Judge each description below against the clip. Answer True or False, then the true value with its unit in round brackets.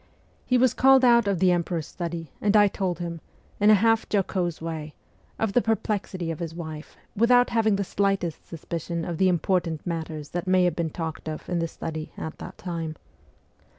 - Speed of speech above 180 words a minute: True (190 wpm)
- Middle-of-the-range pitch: True (175 Hz)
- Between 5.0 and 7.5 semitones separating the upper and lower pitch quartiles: False (3.7 semitones)